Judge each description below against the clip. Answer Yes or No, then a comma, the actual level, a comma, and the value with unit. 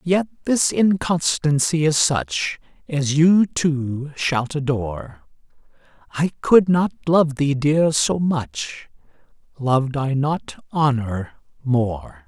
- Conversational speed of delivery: No, slow, 110 wpm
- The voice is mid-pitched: Yes, medium, 145 Hz